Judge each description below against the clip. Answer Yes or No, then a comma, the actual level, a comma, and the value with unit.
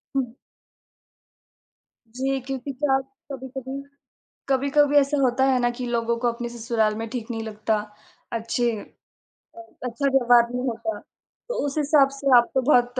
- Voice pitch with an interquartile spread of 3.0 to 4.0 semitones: No, narrow, 2.4 semitones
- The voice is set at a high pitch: Yes, very high, 250 Hz